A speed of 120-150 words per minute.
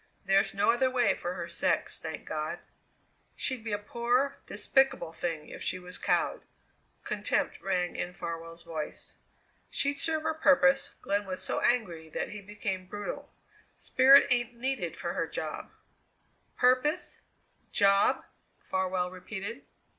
Yes: average, 140 wpm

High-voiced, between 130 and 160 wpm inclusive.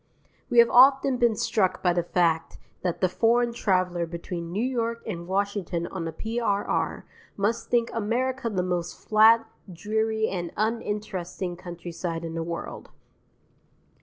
Yes: high, 200 Hz; average, 140 wpm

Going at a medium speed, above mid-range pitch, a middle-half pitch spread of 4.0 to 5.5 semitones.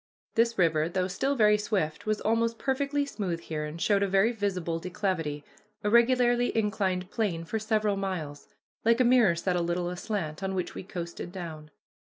Yes: average, 180 wpm; high, 195 Hz; average, 4.7 semitones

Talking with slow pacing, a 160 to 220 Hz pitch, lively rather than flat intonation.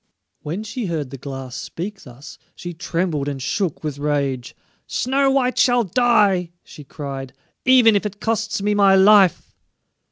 No: average, 155 wpm; medium, 185 Hz; wide, 6.9 semitones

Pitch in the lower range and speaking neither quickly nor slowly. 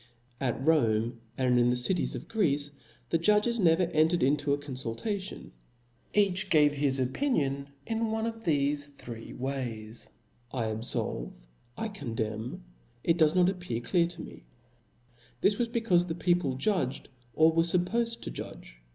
No: medium, 150 Hz; average, 145 wpm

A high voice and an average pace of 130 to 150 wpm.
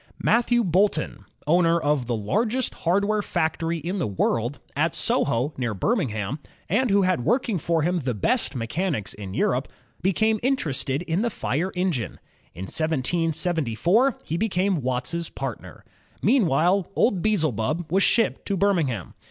No: medium, 170 Hz; average, 140 wpm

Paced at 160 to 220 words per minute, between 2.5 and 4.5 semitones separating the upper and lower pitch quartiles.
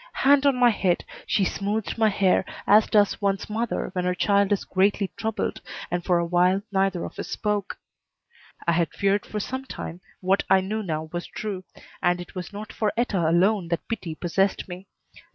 Yes: average, 190 wpm; average, 2.9 semitones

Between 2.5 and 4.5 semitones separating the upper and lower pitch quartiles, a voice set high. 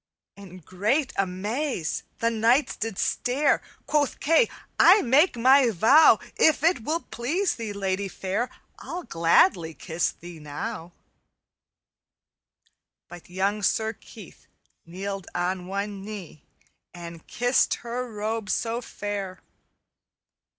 No: average, 4.9 semitones; high, 210 Hz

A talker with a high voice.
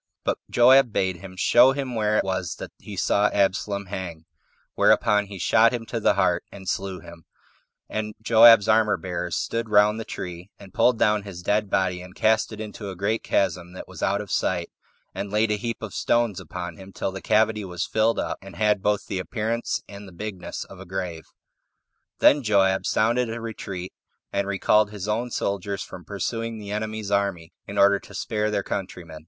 No: low, 100 Hz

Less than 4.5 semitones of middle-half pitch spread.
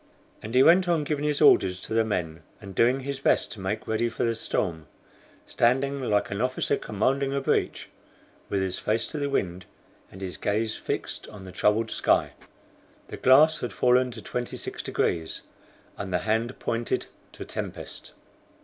No: average, 5.3 semitones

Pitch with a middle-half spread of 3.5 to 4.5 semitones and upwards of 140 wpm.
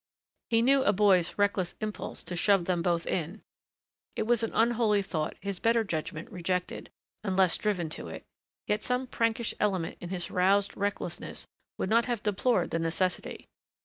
Yes: average, 3.8 semitones; average, 165 wpm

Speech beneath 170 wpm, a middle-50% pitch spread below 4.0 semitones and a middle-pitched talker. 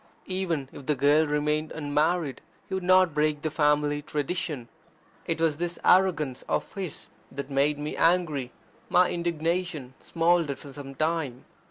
Yes: average, 150 wpm; average, 3.0 semitones; medium, 155 Hz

